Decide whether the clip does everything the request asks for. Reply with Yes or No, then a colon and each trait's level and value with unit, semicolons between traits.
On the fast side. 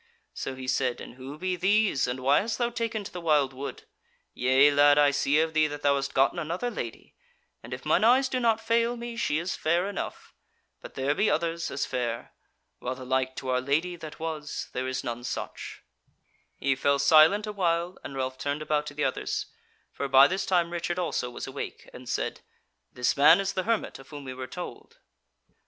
Yes: fast, 210 wpm